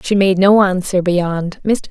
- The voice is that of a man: No, female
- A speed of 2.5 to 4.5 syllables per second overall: Yes, 3.9 syllables/s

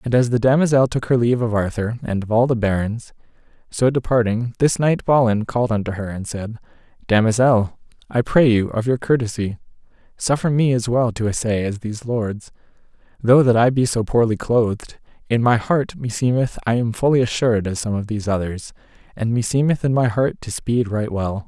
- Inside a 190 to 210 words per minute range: Yes, average, 195 wpm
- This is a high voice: No, low, 115 Hz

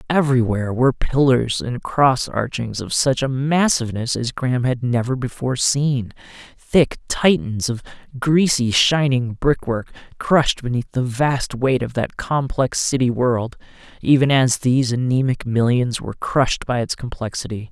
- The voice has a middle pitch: No, low, 125 Hz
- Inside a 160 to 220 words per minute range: No, average, 140 wpm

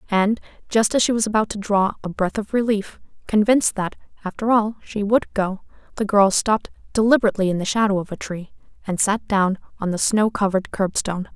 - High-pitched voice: Yes, high, 205 Hz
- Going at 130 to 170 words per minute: No, average, 195 wpm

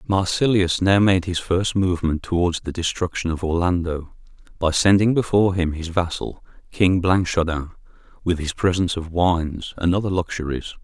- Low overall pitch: Yes, very low, 90 Hz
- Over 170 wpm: No, average, 150 wpm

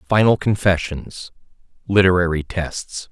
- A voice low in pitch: Yes, very low, 95 Hz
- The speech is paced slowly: Yes, slow, 60 wpm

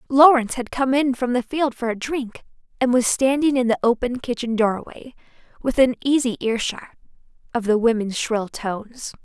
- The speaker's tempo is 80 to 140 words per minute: No, average, 170 wpm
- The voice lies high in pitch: Yes, high, 245 Hz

